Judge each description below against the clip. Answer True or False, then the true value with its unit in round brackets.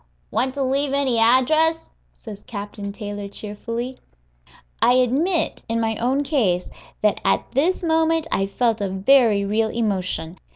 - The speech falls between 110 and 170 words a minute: True (140 wpm)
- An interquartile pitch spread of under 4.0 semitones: False (5.1 semitones)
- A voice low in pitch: False (235 Hz)